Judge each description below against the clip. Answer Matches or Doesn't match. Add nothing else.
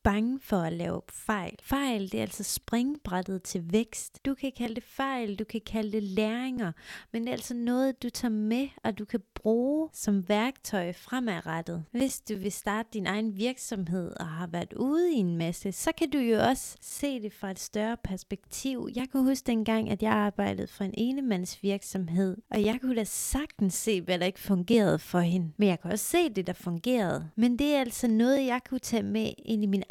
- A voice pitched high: Matches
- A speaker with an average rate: Matches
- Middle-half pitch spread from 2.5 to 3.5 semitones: Doesn't match